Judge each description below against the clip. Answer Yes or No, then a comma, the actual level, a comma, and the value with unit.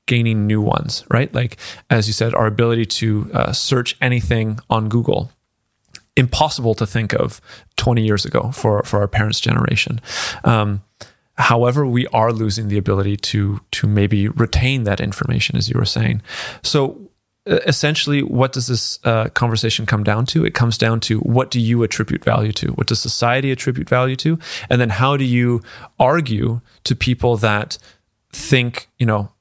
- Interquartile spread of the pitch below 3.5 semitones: Yes, average, 3.0 semitones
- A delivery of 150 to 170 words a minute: Yes, average, 165 wpm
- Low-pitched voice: Yes, low, 115 Hz